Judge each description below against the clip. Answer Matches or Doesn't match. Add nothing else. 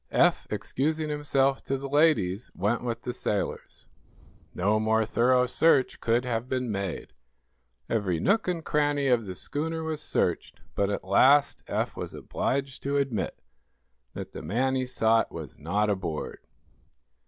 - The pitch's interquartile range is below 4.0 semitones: Doesn't match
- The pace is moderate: Matches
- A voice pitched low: Matches